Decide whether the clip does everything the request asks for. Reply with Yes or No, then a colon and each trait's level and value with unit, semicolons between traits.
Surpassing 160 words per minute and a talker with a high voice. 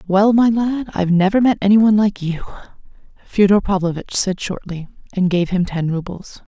Yes: average, 175 wpm; high, 195 Hz